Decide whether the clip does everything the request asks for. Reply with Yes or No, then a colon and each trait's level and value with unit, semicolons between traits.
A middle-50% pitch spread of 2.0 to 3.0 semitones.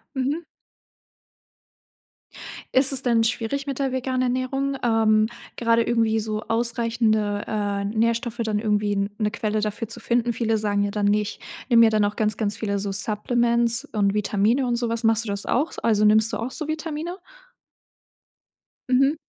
Yes: narrow, 2.6 semitones